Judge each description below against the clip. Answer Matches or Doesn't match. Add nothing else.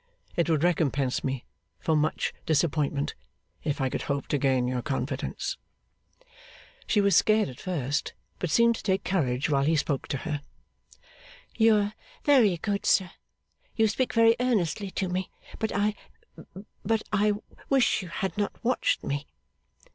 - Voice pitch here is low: Doesn't match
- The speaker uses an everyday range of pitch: Doesn't match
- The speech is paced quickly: Doesn't match